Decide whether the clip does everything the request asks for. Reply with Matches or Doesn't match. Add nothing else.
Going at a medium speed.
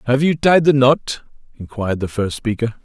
Matches